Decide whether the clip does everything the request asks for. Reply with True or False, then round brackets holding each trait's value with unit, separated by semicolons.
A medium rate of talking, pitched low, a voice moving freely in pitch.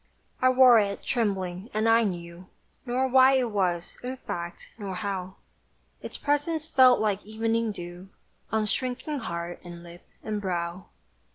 False (150 wpm; 210 Hz; 5.7 semitones)